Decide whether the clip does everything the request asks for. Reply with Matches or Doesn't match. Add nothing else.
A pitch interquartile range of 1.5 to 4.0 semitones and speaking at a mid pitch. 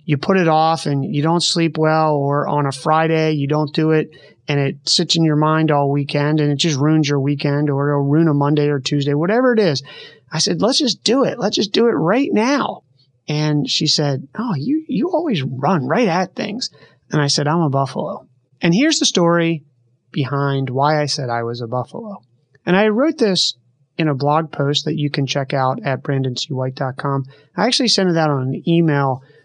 Matches